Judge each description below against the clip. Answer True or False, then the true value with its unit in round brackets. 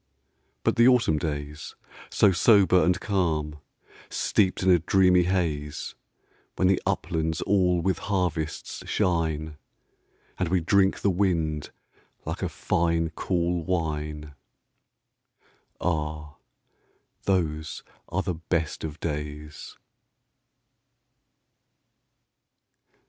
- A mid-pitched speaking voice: False (85 Hz)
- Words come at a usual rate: False (95 wpm)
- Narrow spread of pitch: False (3.2 semitones)